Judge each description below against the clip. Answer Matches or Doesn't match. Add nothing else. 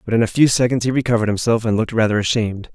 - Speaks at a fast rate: Matches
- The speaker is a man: Matches